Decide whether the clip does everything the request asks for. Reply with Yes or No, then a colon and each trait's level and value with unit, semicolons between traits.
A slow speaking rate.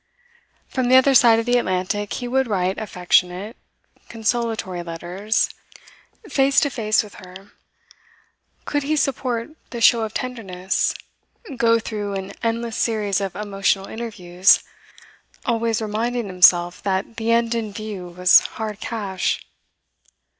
Yes: slow, 130 wpm